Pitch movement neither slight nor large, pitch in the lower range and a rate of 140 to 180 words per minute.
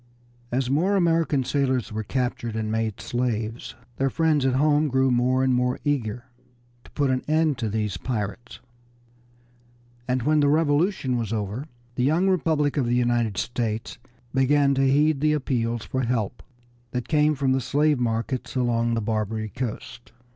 Yes: average, 3.8 semitones; low, 130 Hz; average, 160 wpm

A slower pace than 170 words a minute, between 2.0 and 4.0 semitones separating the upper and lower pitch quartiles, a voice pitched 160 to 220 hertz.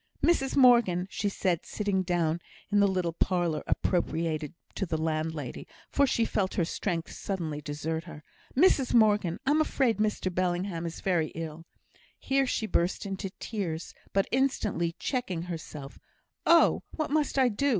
No: average, 150 wpm; average, 5.3 semitones; medium, 185 Hz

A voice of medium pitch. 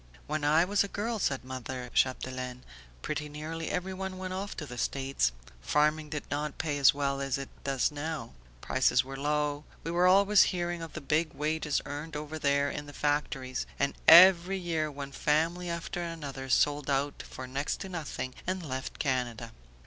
Yes: medium, 150 Hz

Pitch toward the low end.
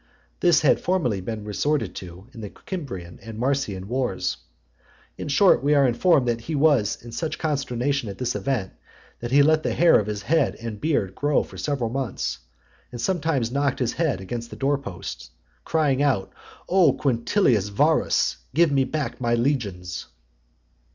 Yes: low, 130 Hz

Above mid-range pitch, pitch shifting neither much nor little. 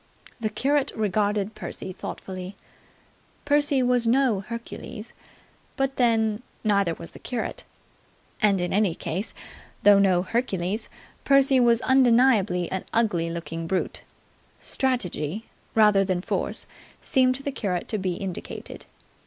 Yes: high, 215 Hz; average, 4.9 semitones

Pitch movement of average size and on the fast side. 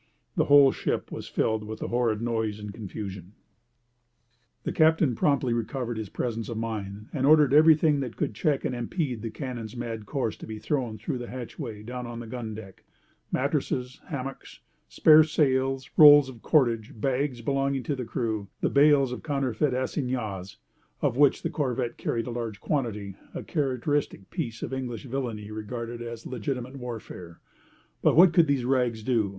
No: average, 3.7 semitones; average, 165 wpm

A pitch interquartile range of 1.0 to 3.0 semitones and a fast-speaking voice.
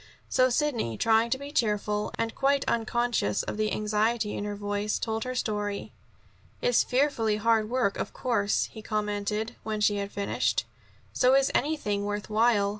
No: average, 2.7 semitones; average, 165 wpm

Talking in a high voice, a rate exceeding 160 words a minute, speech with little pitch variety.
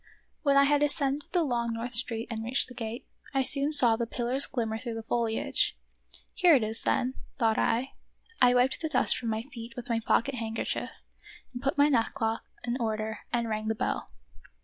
No: high, 240 Hz; average, 195 wpm; average, 3.2 semitones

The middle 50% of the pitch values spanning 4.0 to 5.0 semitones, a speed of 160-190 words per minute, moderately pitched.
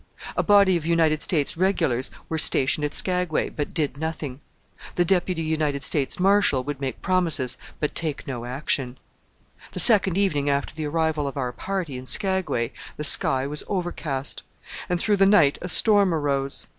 Yes: average, 4.5 semitones; average, 170 wpm; medium, 155 Hz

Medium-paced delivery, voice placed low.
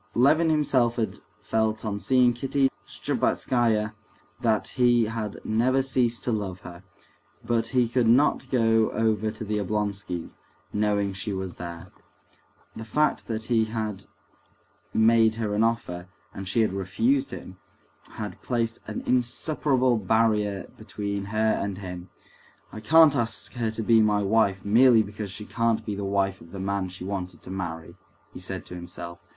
Yes: average, 160 wpm; low, 110 Hz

